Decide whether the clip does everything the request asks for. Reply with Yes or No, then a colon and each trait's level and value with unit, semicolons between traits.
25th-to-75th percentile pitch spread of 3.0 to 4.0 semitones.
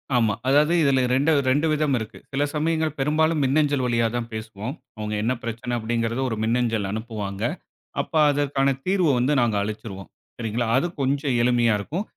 No: average, 4.4 semitones